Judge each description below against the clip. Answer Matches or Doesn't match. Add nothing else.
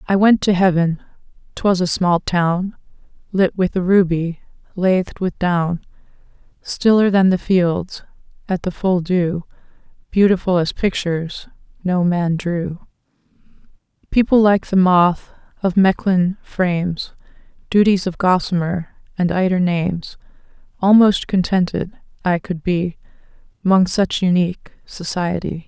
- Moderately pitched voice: Matches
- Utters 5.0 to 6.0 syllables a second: Doesn't match